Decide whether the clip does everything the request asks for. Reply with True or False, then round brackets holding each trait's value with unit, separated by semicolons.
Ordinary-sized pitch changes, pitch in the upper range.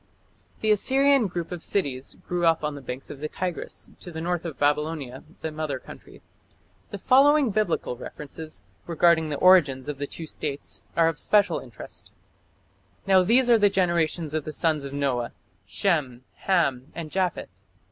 False (4.4 semitones; 165 Hz)